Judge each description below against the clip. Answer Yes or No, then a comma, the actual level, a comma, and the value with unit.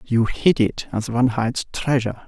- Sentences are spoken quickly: No, average, 185 wpm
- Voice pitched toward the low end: Yes, low, 120 Hz